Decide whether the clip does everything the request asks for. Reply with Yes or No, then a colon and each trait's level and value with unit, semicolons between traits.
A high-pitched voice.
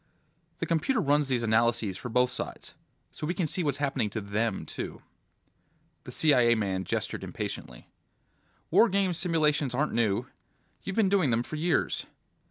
No: medium, 140 Hz